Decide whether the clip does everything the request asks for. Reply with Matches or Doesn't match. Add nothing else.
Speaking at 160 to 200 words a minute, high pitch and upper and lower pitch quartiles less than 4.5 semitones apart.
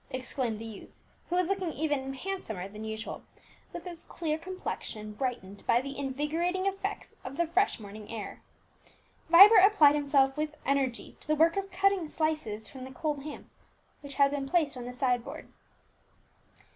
Doesn't match